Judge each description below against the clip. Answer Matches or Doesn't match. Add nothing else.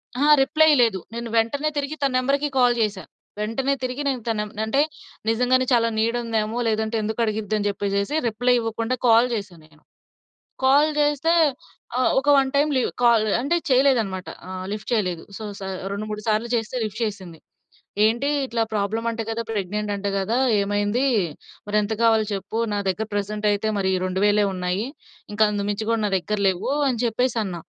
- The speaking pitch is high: Matches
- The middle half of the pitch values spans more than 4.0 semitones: Doesn't match